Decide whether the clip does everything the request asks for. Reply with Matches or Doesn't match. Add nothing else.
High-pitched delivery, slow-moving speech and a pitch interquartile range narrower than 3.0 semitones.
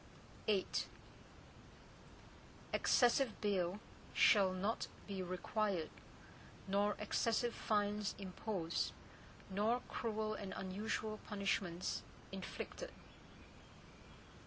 Matches